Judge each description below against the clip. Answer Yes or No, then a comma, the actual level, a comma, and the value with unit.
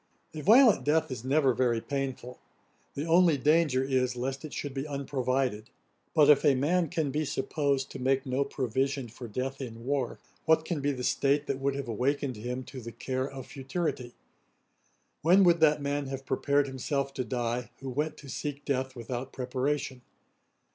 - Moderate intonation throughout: No, narrow, 2.3 semitones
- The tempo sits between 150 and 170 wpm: No, average, 180 wpm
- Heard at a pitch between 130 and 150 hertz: Yes, low, 135 Hz